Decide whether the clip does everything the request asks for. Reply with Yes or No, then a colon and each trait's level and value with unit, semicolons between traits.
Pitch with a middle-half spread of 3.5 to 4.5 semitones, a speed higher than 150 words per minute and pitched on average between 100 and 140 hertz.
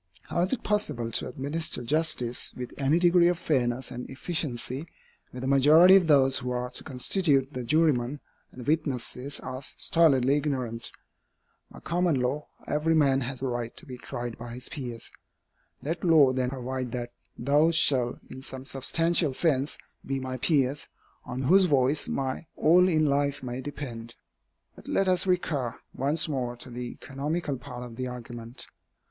Yes: average, 3.9 semitones; average, 165 wpm; low, 135 Hz